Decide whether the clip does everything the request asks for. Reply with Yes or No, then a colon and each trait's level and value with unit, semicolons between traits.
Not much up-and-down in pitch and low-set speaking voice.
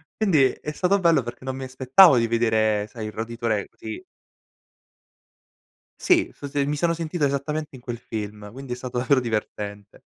No: average, 4.6 semitones; low, 125 Hz